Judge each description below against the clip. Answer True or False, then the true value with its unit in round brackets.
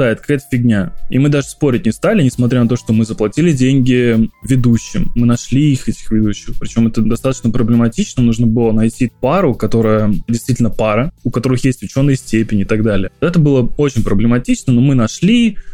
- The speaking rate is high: True (180 wpm)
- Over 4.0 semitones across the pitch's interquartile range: False (3.0 semitones)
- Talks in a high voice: False (120 Hz)